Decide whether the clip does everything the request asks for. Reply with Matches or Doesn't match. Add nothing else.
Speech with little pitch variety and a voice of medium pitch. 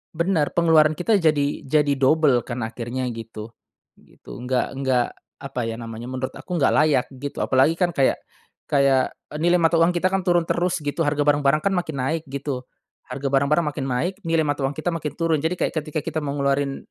Doesn't match